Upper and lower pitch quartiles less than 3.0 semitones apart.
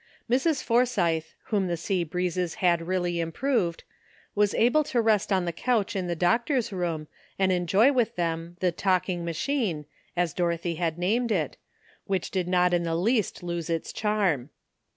No: average, 4.0 semitones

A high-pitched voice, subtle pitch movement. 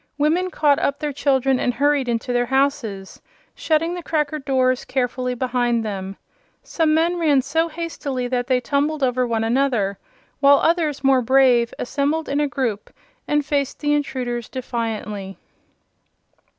No: very high, 270 Hz; average, 3.3 semitones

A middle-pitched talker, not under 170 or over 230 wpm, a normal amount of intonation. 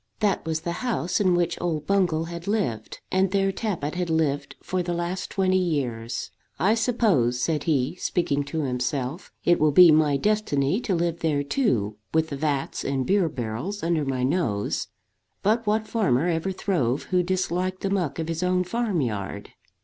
Yes: medium, 170 Hz; average, 180 wpm; average, 4.8 semitones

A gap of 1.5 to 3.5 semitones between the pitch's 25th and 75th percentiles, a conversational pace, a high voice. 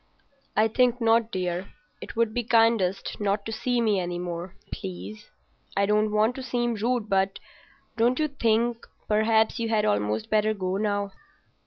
Yes: average, 2.9 semitones; average, 155 wpm; high, 215 Hz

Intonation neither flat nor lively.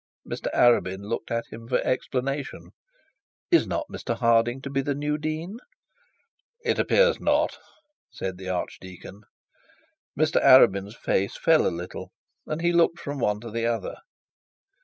No: wide, 6.3 semitones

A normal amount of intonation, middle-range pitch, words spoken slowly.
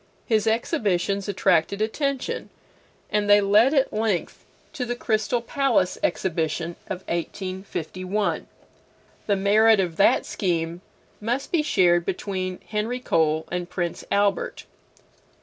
No: average, 3.7 semitones; high, 200 Hz; slow, 115 wpm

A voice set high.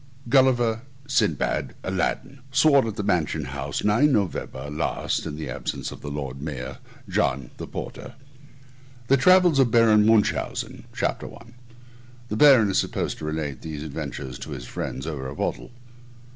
No: low, 100 Hz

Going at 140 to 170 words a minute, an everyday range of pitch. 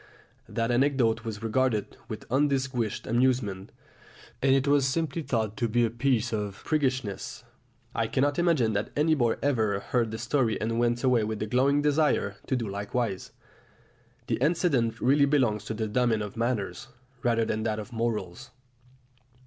Yes: average, 165 wpm; average, 3.6 semitones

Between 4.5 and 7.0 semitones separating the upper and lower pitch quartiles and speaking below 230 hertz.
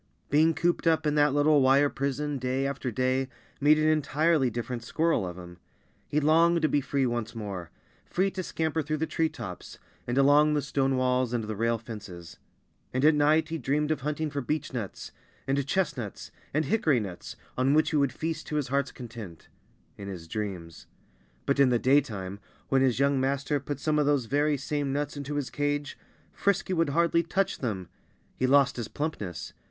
No: average, 3.8 semitones; medium, 140 Hz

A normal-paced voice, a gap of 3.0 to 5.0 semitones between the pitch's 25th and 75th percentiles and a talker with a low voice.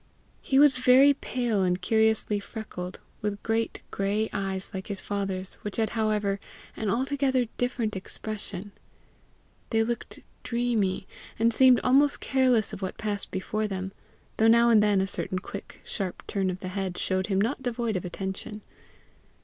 No: average, 155 wpm; average, 3.5 semitones; high, 215 Hz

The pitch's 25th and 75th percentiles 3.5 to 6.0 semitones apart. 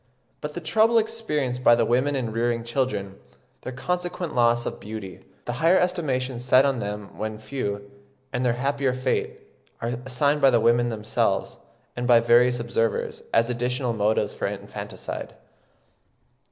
No: average, 3.1 semitones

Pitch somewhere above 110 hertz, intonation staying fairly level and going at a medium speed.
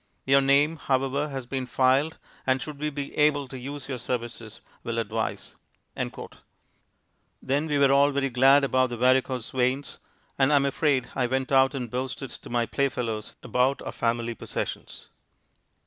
Yes: low, 135 Hz; narrow, 2.0 semitones; average, 165 wpm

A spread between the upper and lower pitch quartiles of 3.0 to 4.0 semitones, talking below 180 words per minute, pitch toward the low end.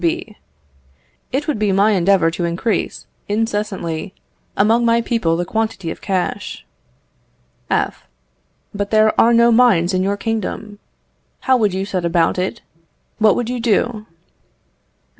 No: average, 3.6 semitones; average, 140 wpm; high, 210 Hz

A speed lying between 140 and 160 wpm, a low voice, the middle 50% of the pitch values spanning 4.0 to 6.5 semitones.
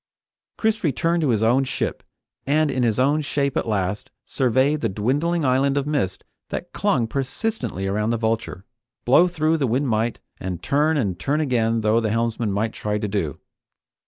No: average, 180 wpm; low, 125 Hz; average, 5.2 semitones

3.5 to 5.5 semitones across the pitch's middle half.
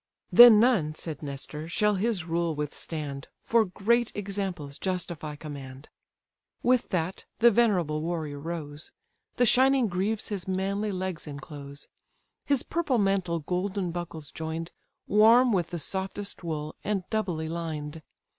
Yes: average, 5.1 semitones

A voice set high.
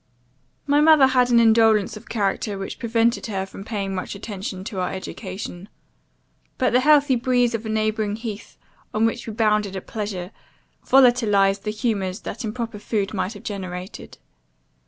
Yes: high, 215 Hz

